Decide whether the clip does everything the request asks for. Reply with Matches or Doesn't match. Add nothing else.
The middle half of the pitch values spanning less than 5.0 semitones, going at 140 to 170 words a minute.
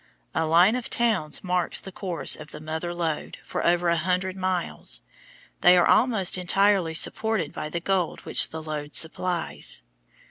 Matches